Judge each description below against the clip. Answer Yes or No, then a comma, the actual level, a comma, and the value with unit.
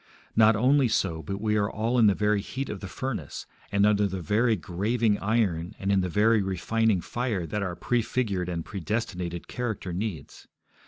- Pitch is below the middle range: Yes, low, 105 Hz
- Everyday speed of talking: Yes, average, 180 wpm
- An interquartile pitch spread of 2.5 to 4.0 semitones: Yes, average, 3.4 semitones